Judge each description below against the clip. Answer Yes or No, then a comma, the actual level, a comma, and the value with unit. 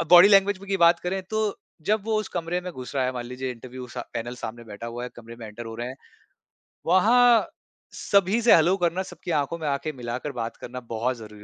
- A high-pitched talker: No, medium, 140 Hz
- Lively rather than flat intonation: Yes, wide, 7.7 semitones